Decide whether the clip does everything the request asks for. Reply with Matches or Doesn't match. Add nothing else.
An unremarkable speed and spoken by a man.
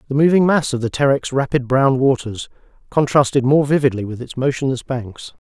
Matches